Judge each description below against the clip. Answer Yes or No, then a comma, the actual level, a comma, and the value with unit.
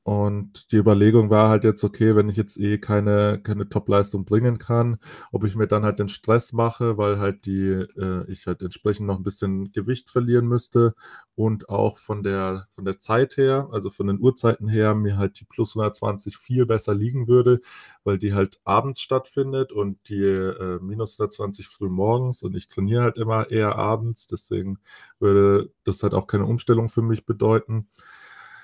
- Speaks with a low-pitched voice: Yes, low, 105 Hz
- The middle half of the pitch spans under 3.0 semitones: Yes, narrow, 2.5 semitones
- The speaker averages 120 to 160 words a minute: No, average, 185 wpm